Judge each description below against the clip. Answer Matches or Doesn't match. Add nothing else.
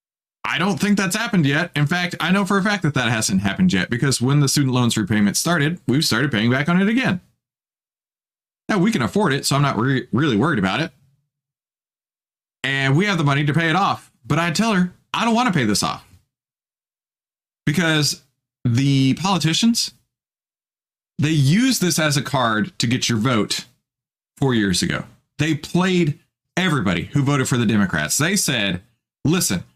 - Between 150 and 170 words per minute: Doesn't match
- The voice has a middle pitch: Matches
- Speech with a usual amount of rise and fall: Doesn't match